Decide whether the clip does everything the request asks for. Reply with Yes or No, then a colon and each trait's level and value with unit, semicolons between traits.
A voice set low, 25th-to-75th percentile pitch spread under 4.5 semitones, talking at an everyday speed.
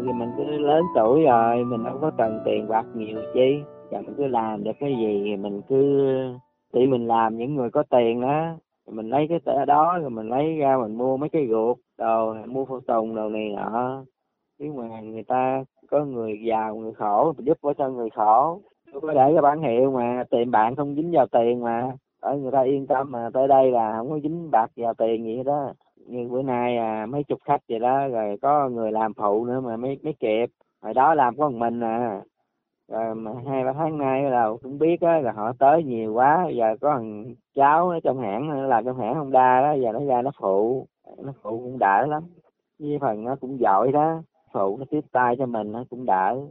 Yes: low, 125 Hz; average, 3.9 semitones; average, 230 wpm